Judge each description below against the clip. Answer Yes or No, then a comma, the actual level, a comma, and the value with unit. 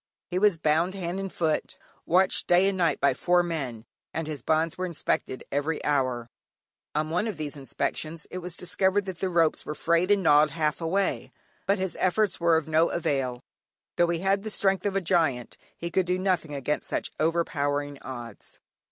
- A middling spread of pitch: Yes, average, 3.6 semitones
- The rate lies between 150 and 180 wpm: No, average, 190 wpm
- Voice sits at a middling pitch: Yes, medium, 165 Hz